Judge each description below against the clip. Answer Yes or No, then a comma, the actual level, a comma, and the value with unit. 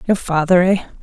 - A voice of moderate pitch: Yes, medium, 180 Hz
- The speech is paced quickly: No, average, 175 wpm